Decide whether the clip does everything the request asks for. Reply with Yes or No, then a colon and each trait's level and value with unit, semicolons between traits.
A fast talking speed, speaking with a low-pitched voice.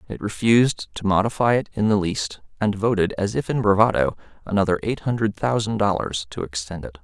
No: average, 190 wpm; low, 100 Hz